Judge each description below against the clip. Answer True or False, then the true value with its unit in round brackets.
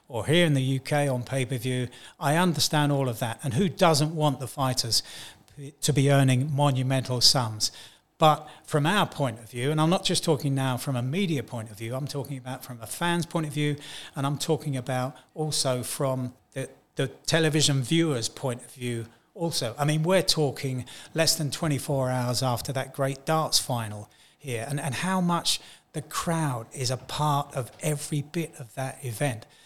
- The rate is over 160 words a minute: True (190 wpm)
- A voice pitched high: False (140 Hz)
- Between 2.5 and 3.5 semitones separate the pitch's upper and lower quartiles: True (3.2 semitones)